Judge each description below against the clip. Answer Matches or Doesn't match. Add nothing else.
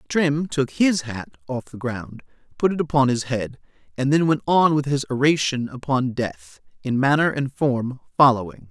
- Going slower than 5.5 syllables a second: Matches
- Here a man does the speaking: Matches